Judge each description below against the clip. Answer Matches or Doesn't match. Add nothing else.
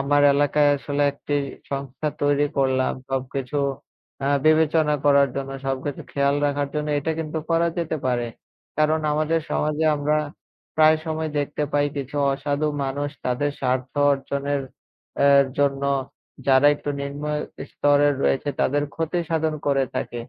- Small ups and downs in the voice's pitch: Matches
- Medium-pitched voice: Matches